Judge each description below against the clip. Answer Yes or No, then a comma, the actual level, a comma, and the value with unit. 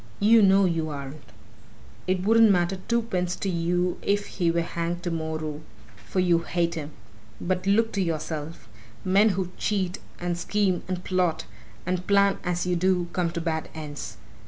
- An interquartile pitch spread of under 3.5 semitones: Yes, narrow, 2.4 semitones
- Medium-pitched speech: Yes, medium, 180 Hz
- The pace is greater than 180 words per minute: No, average, 160 wpm